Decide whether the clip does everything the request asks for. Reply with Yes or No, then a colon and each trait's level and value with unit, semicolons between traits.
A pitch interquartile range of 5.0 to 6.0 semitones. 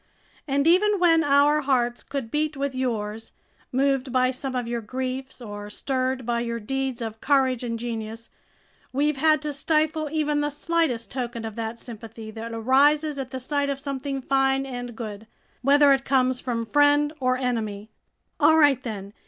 No: average, 3.5 semitones